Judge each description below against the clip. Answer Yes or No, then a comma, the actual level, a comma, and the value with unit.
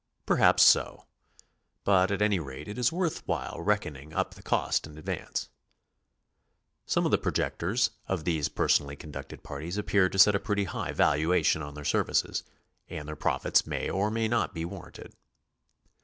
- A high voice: No, very low, 90 Hz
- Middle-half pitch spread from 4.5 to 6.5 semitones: Yes, average, 5.1 semitones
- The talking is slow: No, average, 170 wpm